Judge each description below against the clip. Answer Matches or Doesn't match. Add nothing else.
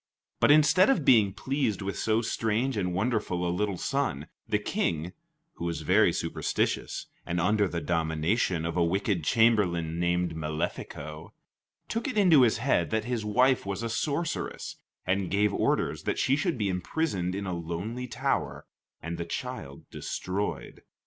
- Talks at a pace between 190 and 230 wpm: Doesn't match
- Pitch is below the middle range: Matches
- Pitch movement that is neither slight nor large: Doesn't match